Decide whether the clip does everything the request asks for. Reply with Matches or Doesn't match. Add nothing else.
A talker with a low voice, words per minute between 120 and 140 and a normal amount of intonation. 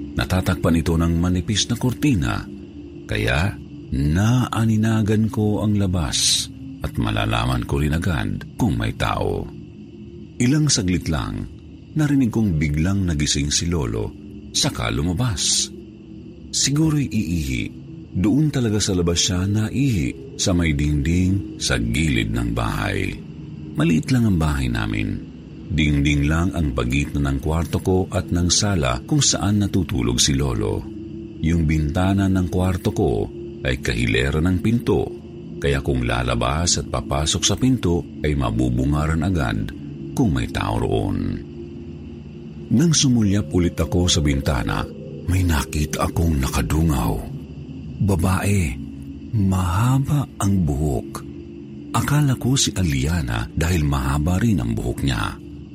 Doesn't match